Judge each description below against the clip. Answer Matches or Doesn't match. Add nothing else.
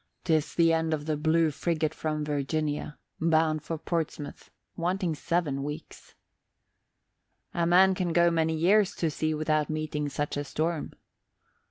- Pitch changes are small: Matches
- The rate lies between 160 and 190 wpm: Doesn't match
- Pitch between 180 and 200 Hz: Doesn't match